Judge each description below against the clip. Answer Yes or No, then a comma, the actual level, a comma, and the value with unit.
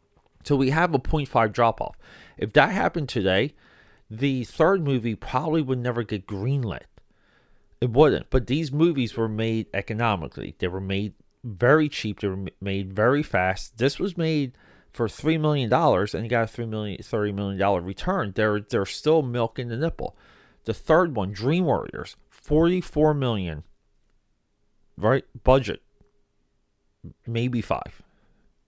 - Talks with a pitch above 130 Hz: No, low, 115 Hz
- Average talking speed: Yes, average, 145 wpm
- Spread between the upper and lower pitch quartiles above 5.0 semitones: Yes, wide, 5.5 semitones